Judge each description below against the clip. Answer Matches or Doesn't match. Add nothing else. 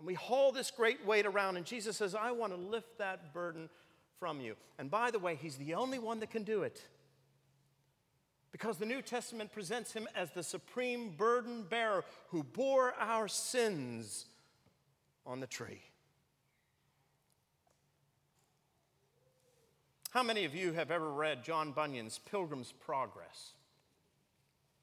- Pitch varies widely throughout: Matches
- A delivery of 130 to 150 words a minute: Matches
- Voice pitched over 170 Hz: Matches